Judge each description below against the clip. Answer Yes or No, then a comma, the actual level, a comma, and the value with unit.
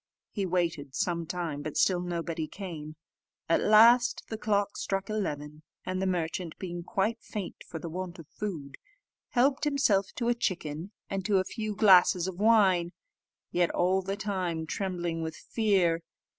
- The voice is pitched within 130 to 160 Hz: No, medium, 185 Hz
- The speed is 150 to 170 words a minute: Yes, average, 160 wpm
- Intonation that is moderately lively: Yes, average, 3.4 semitones